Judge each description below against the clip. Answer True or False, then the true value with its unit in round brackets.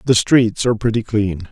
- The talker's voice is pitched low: True (110 Hz)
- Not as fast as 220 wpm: True (200 wpm)